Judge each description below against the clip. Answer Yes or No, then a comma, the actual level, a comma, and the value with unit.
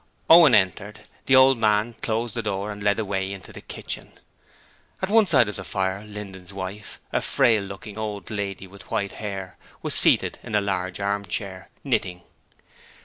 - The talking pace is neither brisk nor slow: Yes, average, 175 wpm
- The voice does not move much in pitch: Yes, narrow, 2.2 semitones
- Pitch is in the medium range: No, low, 100 Hz